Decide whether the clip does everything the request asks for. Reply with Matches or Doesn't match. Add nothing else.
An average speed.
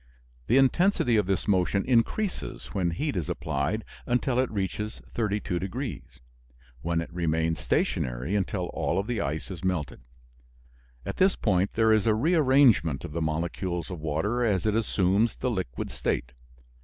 Matches